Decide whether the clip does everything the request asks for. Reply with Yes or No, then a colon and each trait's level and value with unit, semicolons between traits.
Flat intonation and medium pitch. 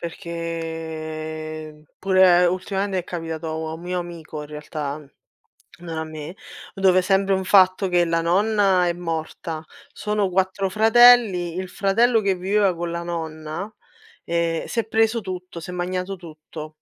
No: average, 3.0 semitones; medium, 175 Hz